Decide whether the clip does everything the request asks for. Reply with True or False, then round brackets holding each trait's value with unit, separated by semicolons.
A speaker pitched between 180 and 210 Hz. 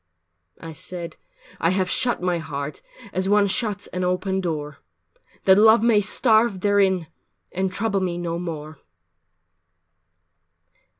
True (185 Hz)